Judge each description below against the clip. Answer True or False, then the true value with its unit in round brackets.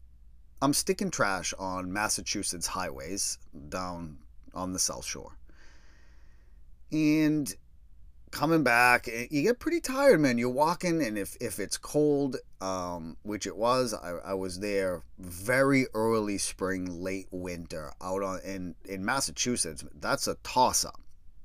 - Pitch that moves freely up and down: True (6.9 semitones)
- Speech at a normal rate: False (130 wpm)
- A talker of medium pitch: False (95 Hz)